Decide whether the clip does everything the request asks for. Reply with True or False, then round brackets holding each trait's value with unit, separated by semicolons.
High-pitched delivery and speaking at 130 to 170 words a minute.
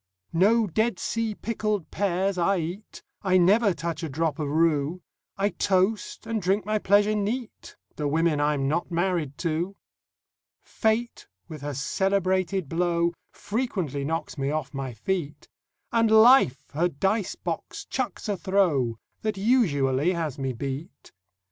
False (180 Hz; 140 wpm)